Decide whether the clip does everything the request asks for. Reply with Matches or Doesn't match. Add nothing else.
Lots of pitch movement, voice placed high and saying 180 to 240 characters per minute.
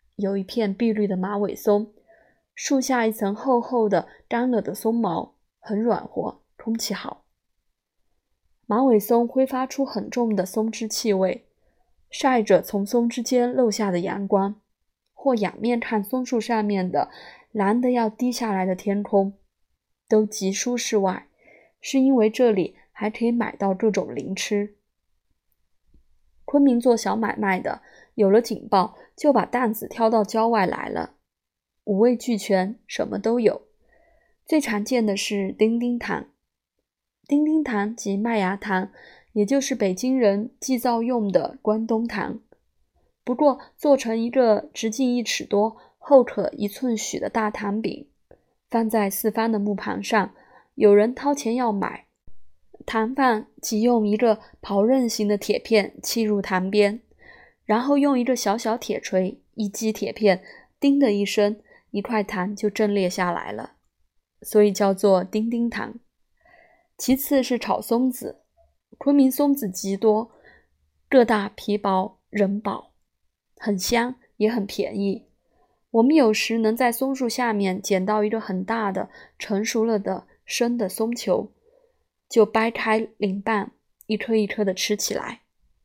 Doesn't match